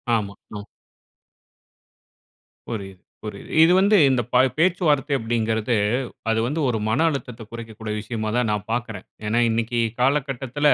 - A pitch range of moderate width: Yes, average, 3.8 semitones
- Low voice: Yes, low, 115 Hz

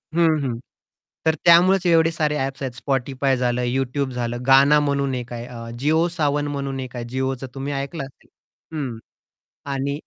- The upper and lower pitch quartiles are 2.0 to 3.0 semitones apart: Yes, average, 2.7 semitones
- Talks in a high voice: No, low, 135 Hz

